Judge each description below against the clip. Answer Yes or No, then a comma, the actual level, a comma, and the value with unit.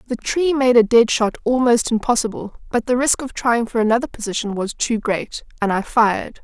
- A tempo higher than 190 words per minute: Yes, fast, 205 wpm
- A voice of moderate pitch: No, high, 235 Hz